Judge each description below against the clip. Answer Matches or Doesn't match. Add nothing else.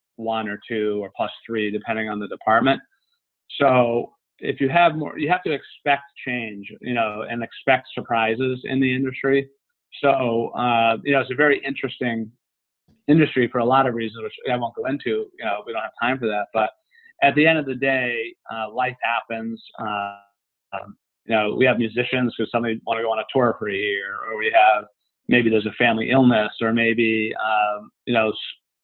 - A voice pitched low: Matches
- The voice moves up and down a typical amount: Matches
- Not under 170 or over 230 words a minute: Matches